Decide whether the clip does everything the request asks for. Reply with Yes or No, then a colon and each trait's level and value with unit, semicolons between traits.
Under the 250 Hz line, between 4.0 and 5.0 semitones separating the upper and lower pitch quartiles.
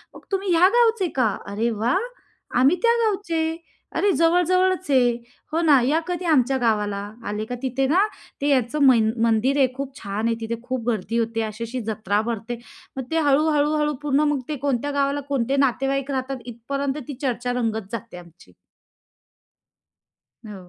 No: very high, 265 Hz; average, 4.5 semitones